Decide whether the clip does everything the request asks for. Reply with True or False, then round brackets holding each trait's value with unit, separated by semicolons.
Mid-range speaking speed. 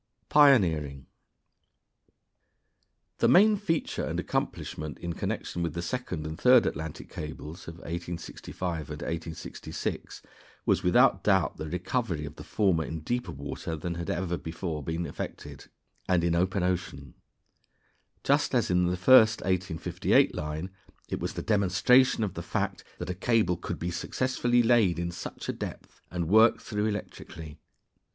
True (150 wpm)